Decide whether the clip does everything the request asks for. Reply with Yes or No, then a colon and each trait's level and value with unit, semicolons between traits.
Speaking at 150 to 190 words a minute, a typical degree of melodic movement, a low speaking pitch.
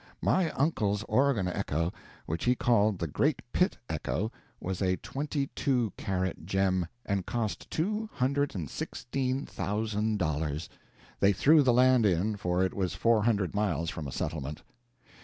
No: average, 155 wpm; wide, 5.7 semitones; low, 105 Hz